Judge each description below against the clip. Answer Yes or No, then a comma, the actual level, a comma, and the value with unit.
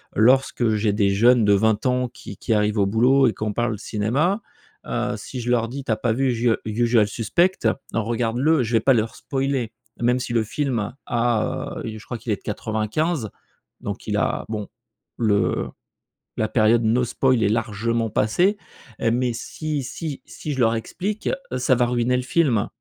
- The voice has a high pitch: No, low, 115 Hz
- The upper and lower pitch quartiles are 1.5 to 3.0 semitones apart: Yes, average, 2.7 semitones